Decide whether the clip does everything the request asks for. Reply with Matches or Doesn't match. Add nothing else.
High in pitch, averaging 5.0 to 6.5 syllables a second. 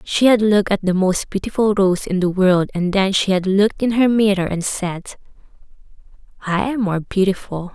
Matches